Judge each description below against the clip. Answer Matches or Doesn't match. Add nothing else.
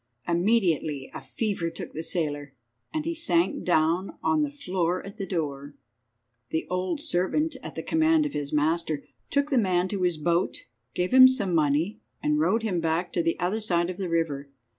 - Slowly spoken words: Doesn't match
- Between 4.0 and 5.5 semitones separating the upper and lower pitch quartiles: Matches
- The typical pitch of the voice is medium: Matches